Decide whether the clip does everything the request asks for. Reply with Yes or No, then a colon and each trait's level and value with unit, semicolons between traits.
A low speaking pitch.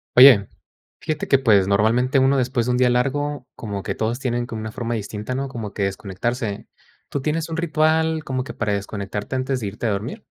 Yes: low, 125 Hz